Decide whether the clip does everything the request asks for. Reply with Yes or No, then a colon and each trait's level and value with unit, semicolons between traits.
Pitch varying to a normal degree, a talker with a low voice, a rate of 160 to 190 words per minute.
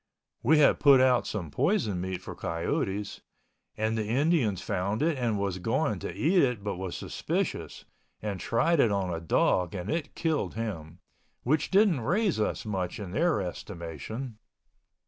No: wide, 7.3 semitones; low, 110 Hz; average, 165 wpm